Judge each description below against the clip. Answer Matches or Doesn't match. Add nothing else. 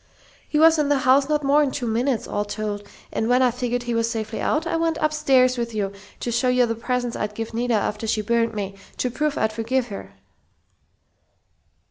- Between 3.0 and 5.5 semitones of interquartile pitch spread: Matches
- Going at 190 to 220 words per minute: Matches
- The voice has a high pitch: Matches